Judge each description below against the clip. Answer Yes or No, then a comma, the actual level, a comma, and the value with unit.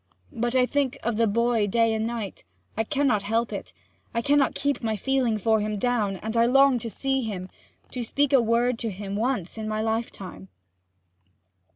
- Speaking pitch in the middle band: No, high, 230 Hz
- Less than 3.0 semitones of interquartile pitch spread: Yes, narrow, 2.6 semitones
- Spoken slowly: No, average, 190 wpm